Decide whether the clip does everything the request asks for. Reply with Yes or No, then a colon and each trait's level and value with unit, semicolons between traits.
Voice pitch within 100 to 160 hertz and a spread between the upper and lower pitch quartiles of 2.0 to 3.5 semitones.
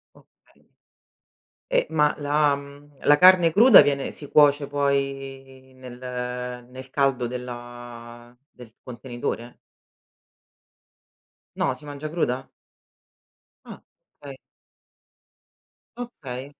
Yes: low, 135 Hz; average, 2.7 semitones